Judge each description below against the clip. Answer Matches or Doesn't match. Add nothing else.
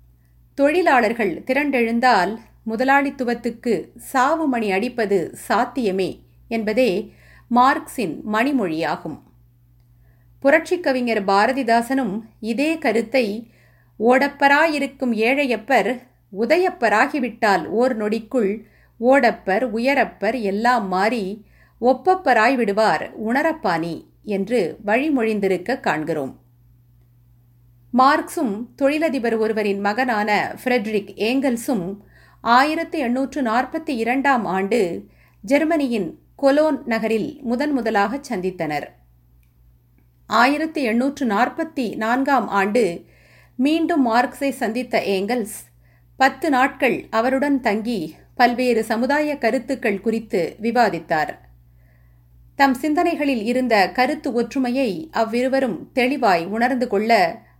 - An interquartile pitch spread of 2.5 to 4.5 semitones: Doesn't match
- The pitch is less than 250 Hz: Matches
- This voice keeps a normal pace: Doesn't match